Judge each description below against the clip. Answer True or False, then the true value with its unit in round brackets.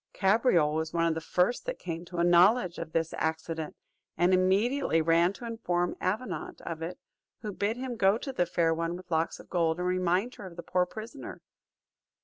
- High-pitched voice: False (180 Hz)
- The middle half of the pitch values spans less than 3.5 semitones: False (3.9 semitones)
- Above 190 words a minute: True (200 wpm)